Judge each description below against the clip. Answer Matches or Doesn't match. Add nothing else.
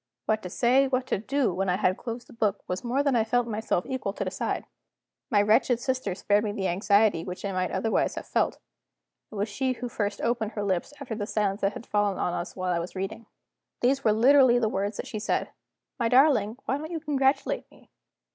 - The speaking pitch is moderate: Doesn't match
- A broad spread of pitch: Doesn't match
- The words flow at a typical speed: Doesn't match